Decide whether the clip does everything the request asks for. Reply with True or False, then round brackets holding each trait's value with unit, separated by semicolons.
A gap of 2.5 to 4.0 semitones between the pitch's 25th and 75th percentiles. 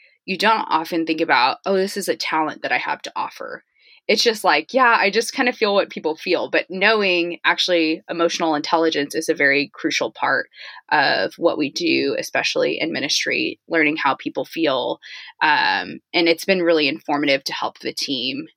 False (5.3 semitones)